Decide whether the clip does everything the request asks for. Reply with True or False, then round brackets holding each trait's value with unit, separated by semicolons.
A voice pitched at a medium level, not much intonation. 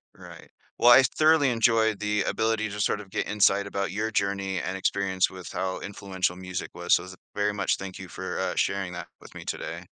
False (100 Hz; 2.3 semitones)